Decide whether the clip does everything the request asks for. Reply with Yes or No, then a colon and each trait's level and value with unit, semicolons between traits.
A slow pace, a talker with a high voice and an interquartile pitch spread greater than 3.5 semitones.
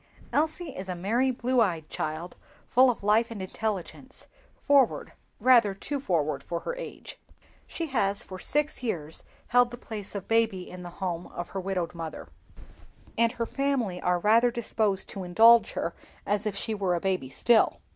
No: average, 170 wpm; high, 210 Hz; average, 5.0 semitones